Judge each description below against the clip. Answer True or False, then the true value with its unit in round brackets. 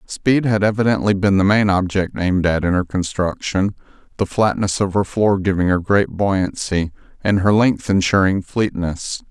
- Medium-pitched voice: False (95 Hz)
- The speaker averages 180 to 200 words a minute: False (170 wpm)